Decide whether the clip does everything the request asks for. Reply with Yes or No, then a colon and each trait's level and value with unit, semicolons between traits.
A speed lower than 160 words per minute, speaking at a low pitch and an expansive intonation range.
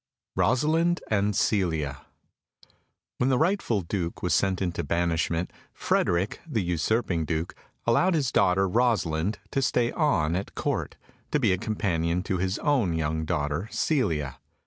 Yes: average, 140 wpm; very low, 95 Hz; wide, 6.2 semitones